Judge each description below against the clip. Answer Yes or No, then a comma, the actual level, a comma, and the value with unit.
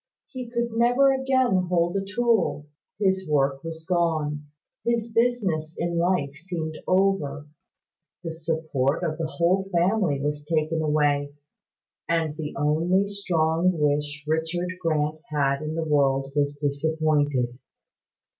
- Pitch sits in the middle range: Yes, medium, 160 Hz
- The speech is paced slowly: Yes, slow, 125 wpm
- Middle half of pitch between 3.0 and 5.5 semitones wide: Yes, average, 4.0 semitones